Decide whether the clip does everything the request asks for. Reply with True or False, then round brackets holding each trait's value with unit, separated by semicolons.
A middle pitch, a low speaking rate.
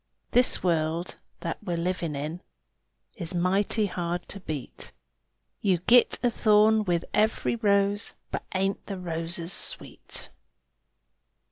True (180 Hz; 125 wpm)